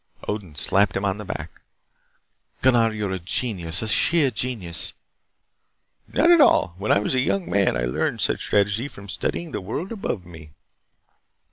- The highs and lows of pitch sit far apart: Yes, wide, 5.8 semitones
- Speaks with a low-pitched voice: Yes, low, 105 Hz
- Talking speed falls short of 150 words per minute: No, average, 170 wpm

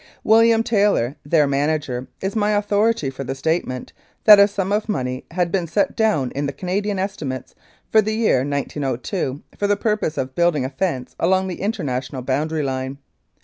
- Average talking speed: Yes, average, 175 wpm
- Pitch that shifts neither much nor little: No, wide, 7.3 semitones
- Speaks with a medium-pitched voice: Yes, medium, 165 Hz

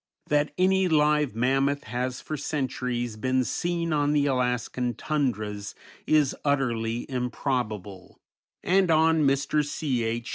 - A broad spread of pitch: No, average, 3.7 semitones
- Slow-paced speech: Yes, slow, 120 wpm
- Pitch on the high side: No, low, 135 Hz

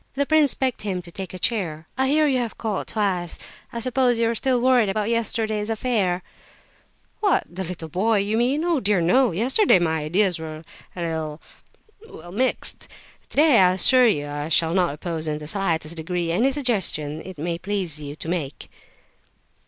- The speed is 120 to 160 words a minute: No, average, 175 wpm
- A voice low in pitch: No, high, 195 Hz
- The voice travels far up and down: Yes, wide, 6.5 semitones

